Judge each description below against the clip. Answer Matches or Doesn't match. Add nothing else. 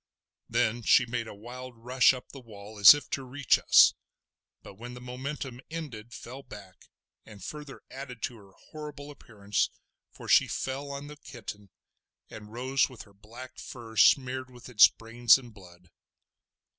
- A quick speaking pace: Doesn't match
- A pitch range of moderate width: Matches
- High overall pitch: Doesn't match